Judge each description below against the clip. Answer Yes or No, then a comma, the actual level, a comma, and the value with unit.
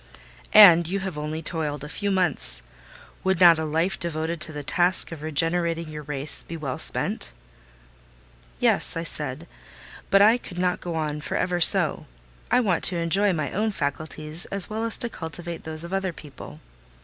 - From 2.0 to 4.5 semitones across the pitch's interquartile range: Yes, average, 3.2 semitones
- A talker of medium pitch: Yes, medium, 165 Hz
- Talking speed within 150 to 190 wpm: Yes, average, 180 wpm